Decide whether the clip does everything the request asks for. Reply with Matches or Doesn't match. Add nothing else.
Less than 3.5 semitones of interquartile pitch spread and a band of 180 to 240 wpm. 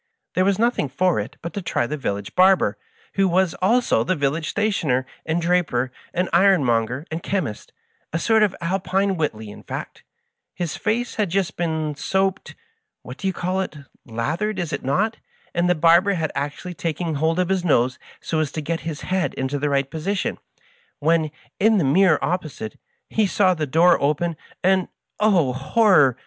Doesn't match